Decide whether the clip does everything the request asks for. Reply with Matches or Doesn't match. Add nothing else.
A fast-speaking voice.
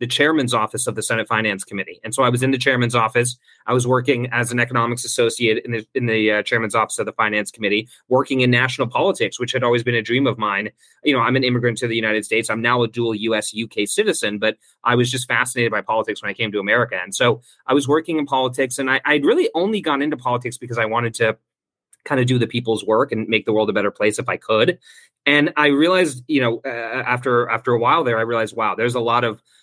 Matches